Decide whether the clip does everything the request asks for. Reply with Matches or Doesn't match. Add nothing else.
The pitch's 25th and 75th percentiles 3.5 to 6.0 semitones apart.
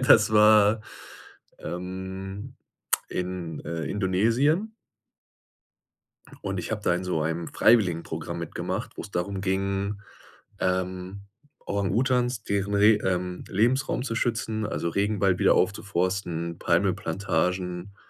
Doesn't match